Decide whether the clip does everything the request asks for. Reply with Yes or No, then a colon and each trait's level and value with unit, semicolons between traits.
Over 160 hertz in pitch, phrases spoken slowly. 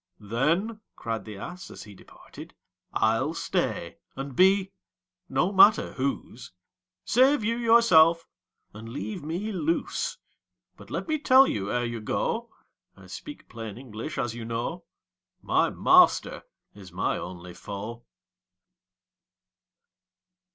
No: medium, 140 Hz; slow, 125 wpm